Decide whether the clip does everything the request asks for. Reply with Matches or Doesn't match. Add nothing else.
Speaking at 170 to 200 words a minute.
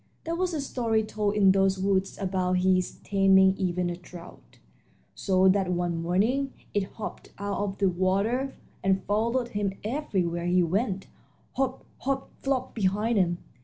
Doesn't match